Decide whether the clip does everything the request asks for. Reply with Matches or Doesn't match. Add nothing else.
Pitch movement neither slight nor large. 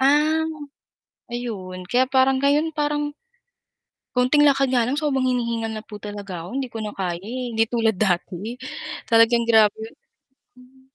Matches